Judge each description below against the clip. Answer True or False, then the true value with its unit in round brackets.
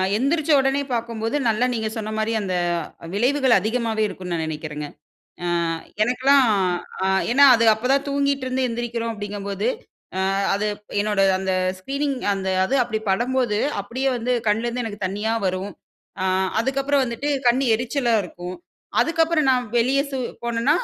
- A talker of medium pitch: False (235 Hz)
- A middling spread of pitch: True (4.4 semitones)